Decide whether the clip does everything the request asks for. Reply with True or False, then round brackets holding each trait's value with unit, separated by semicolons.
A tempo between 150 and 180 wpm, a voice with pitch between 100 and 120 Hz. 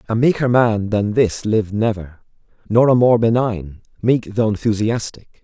True (155 wpm; 110 Hz)